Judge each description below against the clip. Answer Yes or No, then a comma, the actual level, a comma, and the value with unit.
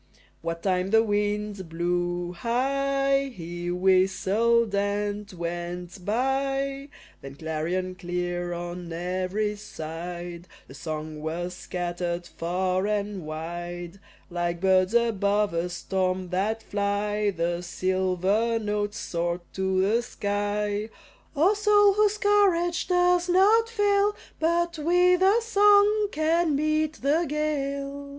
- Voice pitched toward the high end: Yes, high, 205 Hz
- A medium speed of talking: No, slow, 115 wpm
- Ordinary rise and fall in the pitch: No, wide, 7.8 semitones